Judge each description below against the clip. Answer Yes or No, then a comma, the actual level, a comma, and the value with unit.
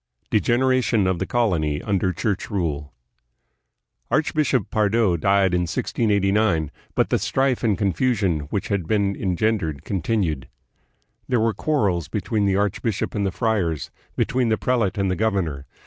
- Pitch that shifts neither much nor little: Yes, average, 4.1 semitones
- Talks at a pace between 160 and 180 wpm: No, average, 145 wpm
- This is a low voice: Yes, low, 100 Hz